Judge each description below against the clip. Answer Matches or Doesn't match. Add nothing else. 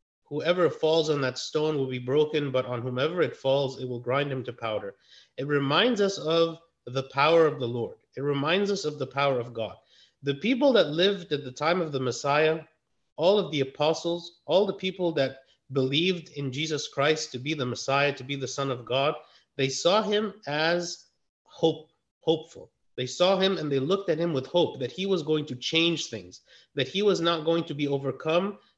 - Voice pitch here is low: Doesn't match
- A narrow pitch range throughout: Doesn't match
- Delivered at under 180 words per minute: Doesn't match